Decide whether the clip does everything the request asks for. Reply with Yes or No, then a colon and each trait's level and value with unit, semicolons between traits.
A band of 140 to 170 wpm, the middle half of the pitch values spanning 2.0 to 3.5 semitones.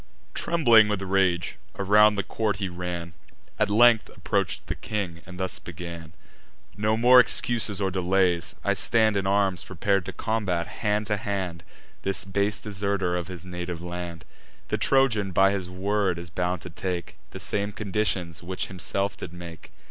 Yes: average, 165 wpm; average, 2.9 semitones